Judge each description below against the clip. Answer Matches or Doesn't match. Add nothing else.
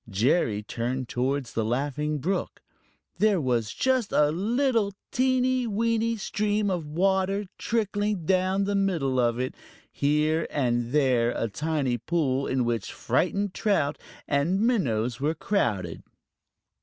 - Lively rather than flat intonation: Matches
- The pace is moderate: Doesn't match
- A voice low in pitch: Doesn't match